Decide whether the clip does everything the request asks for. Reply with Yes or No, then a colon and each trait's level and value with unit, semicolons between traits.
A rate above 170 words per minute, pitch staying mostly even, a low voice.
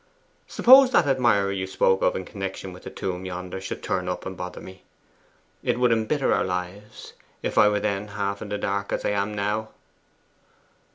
Yes: average, 190 wpm; narrow, 2.1 semitones; low, 100 Hz